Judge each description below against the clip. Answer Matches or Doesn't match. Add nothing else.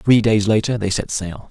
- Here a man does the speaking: Matches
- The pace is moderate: Doesn't match